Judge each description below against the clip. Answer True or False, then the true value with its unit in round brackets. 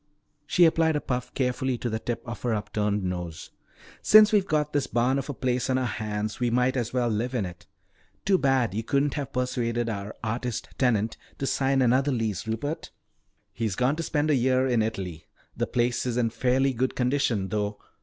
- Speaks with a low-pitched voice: True (125 Hz)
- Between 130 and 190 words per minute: False (200 wpm)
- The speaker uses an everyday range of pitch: True (3.2 semitones)